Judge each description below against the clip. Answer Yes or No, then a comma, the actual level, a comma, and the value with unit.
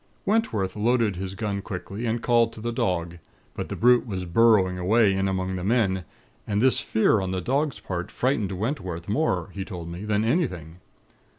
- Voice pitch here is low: Yes, low, 100 Hz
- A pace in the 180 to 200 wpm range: Yes, average, 185 wpm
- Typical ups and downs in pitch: Yes, average, 4.0 semitones